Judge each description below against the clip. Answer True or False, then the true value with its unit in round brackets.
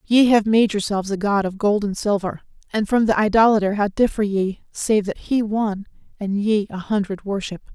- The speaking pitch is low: False (205 Hz)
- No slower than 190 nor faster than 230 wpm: True (200 wpm)